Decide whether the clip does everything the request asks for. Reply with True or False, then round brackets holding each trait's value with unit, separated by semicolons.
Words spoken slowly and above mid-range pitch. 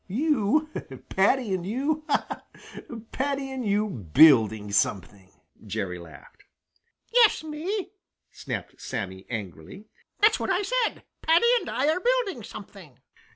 True (125 wpm; 215 Hz)